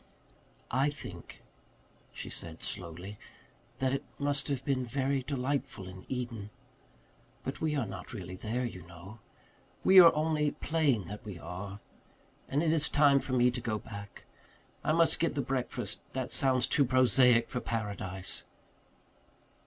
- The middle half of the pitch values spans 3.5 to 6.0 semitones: Yes, wide, 5.6 semitones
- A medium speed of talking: Yes, average, 150 wpm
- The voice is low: Yes, low, 125 Hz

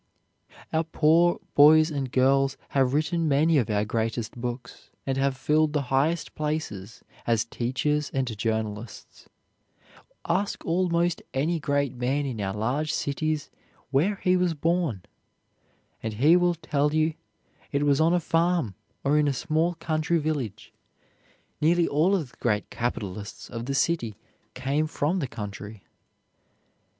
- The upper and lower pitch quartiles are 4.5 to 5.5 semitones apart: Yes, average, 4.8 semitones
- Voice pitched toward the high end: No, medium, 145 Hz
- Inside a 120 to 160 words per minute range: Yes, average, 140 wpm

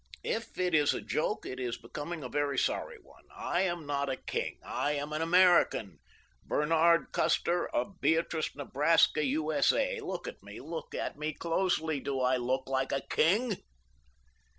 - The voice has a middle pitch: Yes, medium, 155 Hz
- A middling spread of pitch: Yes, average, 3.8 semitones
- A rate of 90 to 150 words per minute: No, average, 160 wpm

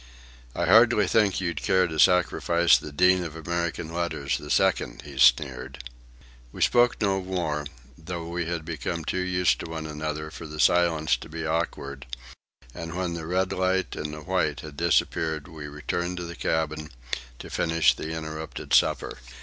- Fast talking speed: No, average, 170 wpm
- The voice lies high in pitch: No, very low, 80 Hz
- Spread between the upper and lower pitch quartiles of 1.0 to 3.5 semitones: Yes, narrow, 2.5 semitones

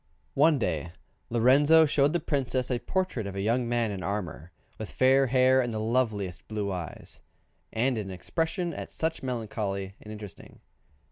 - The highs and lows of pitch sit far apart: No, average, 4.9 semitones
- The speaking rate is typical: Yes, average, 160 wpm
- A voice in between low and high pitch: No, low, 120 Hz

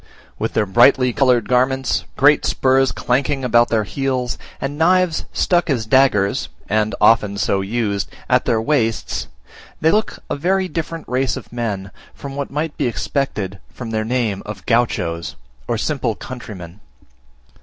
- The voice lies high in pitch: No, low, 125 Hz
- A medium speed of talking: Yes, average, 150 wpm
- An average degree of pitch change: Yes, average, 4.2 semitones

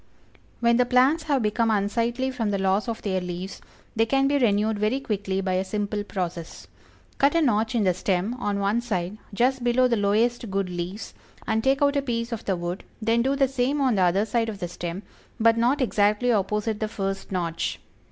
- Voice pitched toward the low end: No, high, 220 Hz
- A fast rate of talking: Yes, fast, 210 wpm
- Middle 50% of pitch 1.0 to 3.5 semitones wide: No, average, 3.9 semitones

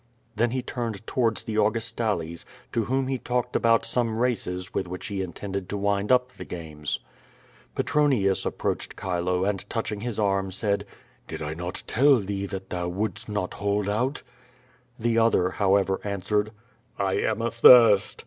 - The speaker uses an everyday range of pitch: Yes, average, 3.4 semitones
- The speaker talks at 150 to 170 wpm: Yes, average, 160 wpm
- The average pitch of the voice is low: Yes, low, 105 Hz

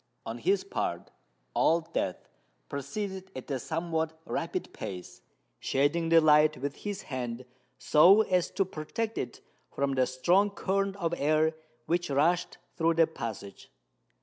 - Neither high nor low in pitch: Yes, medium, 160 Hz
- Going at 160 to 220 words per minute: No, average, 140 wpm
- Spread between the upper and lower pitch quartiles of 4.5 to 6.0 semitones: Yes, average, 4.9 semitones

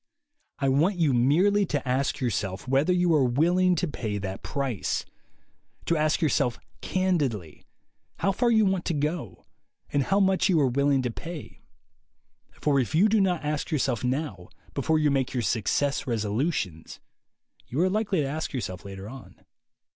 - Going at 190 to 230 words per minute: No, average, 165 wpm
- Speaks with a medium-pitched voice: Yes, medium, 145 Hz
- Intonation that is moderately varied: No, wide, 6.2 semitones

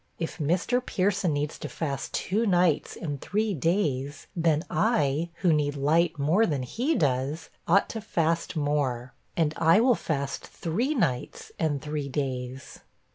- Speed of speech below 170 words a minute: Yes, average, 150 wpm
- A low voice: No, medium, 160 Hz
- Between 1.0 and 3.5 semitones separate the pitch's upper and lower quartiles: No, average, 4.3 semitones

